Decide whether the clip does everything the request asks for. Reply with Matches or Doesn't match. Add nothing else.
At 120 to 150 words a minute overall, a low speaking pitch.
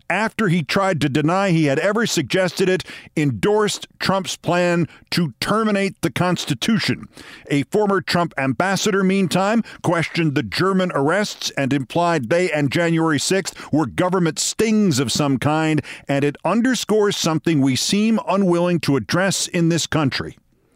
Doesn't match